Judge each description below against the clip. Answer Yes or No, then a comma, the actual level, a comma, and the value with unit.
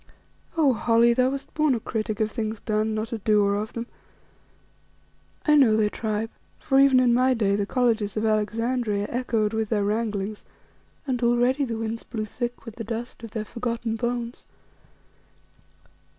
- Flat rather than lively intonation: Yes, narrow, 2.2 semitones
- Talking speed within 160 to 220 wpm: Yes, average, 165 wpm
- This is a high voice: Yes, high, 230 Hz